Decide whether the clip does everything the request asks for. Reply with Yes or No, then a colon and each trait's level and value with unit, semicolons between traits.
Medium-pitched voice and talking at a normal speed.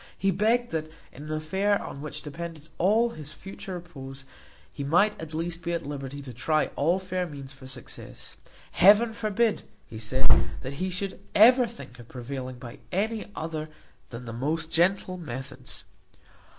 Yes: medium, 160 Hz; average, 165 wpm